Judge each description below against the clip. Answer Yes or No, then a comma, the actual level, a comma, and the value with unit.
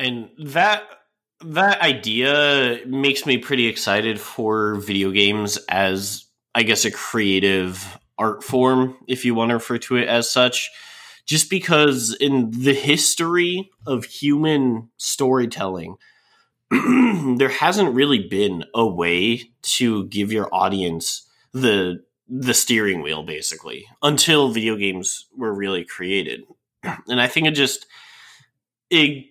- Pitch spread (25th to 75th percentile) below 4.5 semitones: No, average, 5.1 semitones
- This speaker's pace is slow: Yes, slow, 125 wpm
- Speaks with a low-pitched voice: Yes, low, 125 Hz